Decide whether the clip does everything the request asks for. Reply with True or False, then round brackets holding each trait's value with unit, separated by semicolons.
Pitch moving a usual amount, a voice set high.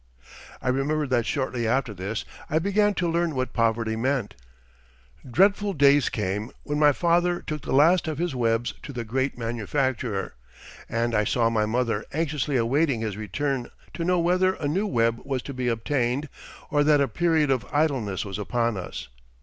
False (4.9 semitones; 130 Hz)